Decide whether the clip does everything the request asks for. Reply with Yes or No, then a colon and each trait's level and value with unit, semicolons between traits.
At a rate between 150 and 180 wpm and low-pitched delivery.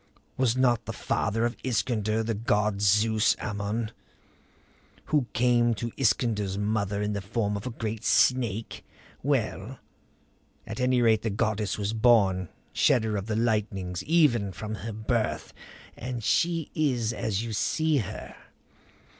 No: average, 140 wpm; low, 110 Hz